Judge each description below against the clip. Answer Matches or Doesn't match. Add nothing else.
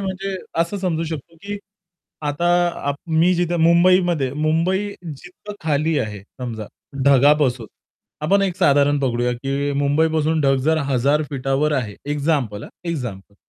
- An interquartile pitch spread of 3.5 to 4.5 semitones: Matches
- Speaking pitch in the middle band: Matches